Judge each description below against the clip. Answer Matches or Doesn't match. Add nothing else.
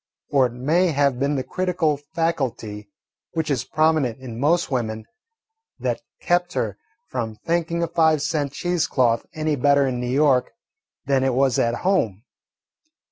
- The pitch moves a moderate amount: Matches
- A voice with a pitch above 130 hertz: Matches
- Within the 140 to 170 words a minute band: Matches